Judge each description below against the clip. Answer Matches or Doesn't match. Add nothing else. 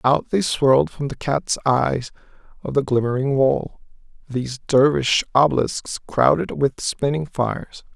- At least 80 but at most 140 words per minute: Matches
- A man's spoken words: Matches